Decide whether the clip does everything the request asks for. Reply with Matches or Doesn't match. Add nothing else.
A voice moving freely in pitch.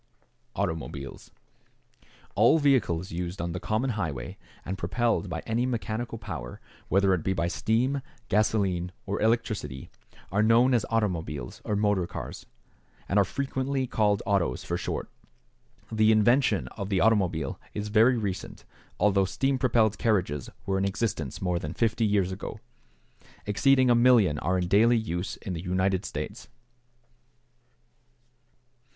Doesn't match